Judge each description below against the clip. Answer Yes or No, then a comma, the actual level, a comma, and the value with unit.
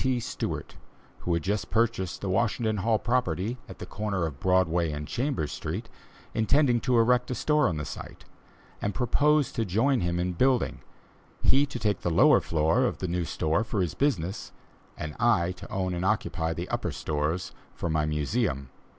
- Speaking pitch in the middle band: No, very low, 95 Hz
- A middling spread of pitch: No, wide, 6.0 semitones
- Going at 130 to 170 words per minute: No, average, 185 wpm